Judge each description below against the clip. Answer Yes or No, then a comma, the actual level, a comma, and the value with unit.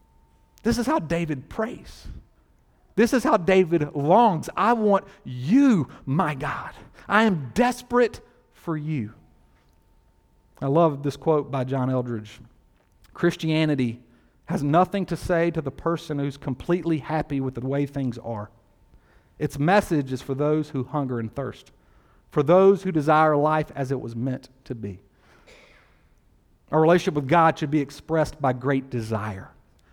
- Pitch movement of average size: No, wide, 5.8 semitones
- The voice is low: No, medium, 145 Hz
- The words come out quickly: No, average, 145 wpm